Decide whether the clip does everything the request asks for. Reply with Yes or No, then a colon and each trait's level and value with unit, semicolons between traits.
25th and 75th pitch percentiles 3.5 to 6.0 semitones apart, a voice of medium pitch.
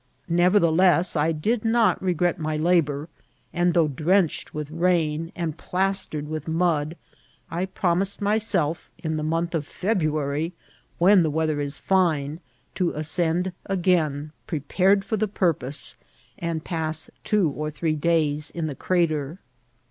No: average, 3.0 semitones; medium, 165 Hz